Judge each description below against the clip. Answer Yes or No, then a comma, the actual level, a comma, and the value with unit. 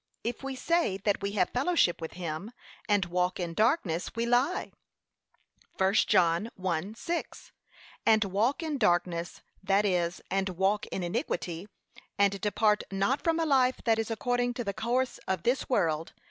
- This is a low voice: No, high, 205 Hz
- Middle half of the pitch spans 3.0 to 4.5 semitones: No, average, 5.2 semitones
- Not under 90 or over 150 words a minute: No, average, 160 wpm